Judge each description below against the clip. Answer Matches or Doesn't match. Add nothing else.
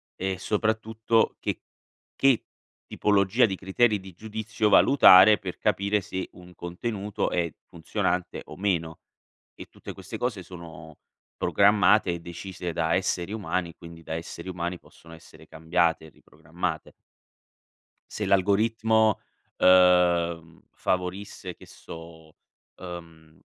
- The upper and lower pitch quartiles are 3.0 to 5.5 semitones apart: Matches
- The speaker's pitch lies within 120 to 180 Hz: Doesn't match